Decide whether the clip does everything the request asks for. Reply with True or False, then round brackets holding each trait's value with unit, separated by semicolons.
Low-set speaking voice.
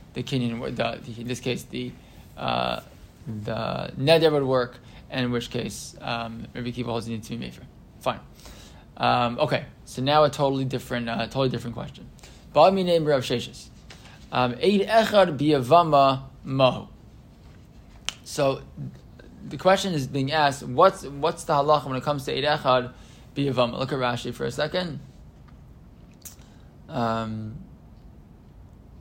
True (125 Hz)